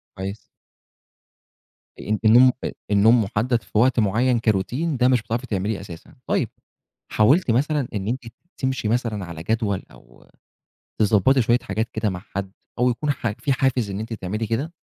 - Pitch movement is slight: No, average, 3.8 semitones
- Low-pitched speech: Yes, low, 115 Hz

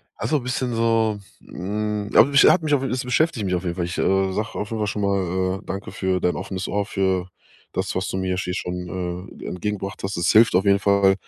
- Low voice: Yes, low, 100 Hz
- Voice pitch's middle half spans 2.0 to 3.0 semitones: Yes, average, 2.7 semitones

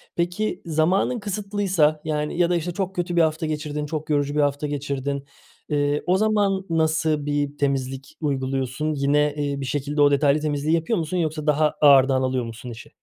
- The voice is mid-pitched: Yes, medium, 150 Hz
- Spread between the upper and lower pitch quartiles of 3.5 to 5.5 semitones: No, average, 2.7 semitones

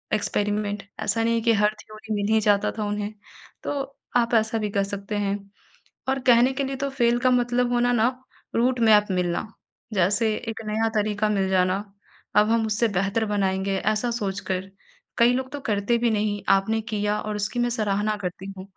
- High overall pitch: Yes, high, 215 Hz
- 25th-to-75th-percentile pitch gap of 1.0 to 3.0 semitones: Yes, narrow, 2.5 semitones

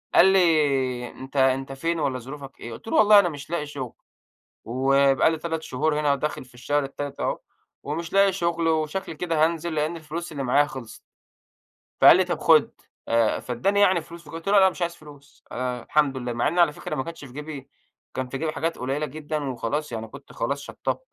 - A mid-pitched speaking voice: Yes, medium, 150 Hz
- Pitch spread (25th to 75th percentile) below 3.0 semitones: No, average, 3.7 semitones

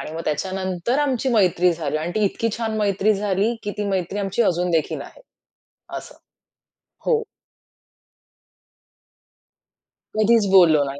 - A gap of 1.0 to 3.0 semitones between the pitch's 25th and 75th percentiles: No, average, 3.8 semitones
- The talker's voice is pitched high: Yes, high, 195 Hz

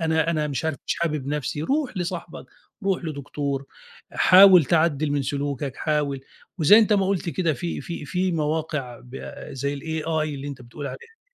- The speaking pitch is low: No, medium, 155 Hz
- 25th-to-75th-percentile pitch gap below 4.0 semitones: Yes, average, 3.3 semitones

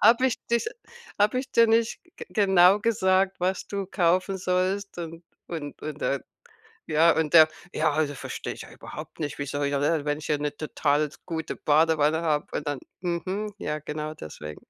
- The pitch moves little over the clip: No, average, 4.4 semitones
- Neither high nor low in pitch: Yes, medium, 165 Hz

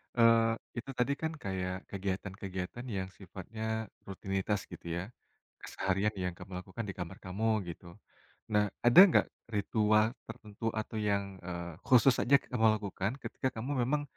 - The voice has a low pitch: Yes, low, 105 Hz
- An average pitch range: Yes, average, 3.2 semitones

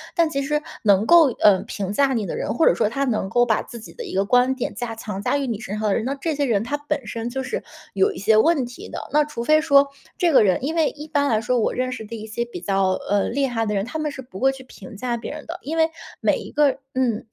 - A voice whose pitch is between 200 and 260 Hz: Yes, high, 245 Hz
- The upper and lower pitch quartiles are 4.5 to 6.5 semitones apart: Yes, average, 4.8 semitones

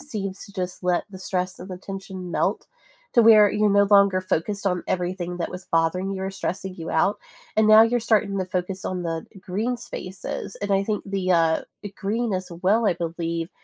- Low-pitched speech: No, high, 190 Hz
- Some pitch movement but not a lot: No, narrow, 2.2 semitones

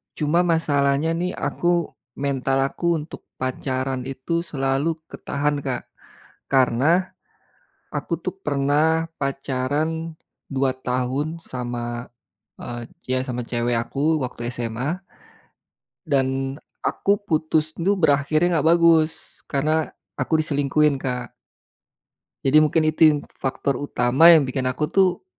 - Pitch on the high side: No, medium, 140 Hz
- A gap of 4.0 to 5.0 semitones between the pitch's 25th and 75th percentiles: No, average, 3.5 semitones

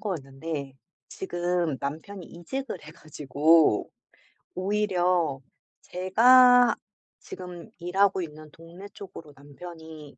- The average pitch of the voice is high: No, medium, 175 Hz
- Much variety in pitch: No, average, 3.7 semitones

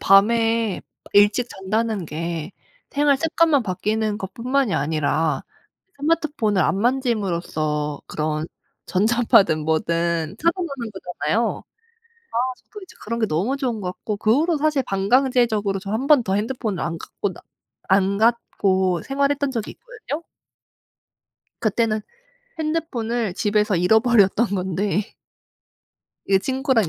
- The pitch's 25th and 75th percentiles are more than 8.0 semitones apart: No, average, 5.2 semitones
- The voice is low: No, high, 215 Hz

